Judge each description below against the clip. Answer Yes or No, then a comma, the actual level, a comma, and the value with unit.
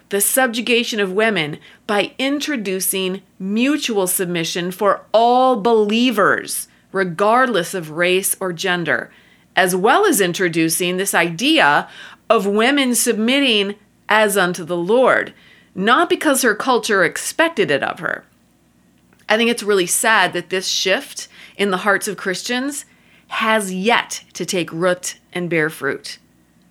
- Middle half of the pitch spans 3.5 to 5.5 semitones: Yes, average, 4.6 semitones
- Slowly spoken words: Yes, slow, 130 wpm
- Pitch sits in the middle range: No, high, 200 Hz